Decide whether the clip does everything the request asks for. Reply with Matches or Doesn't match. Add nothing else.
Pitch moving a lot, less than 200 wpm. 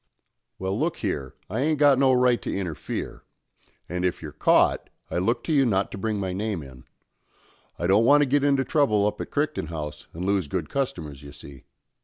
Doesn't match